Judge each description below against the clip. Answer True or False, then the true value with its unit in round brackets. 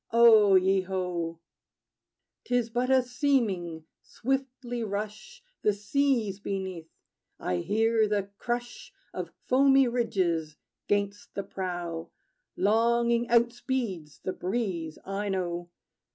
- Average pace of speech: False (110 wpm)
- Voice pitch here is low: False (205 Hz)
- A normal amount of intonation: True (4.5 semitones)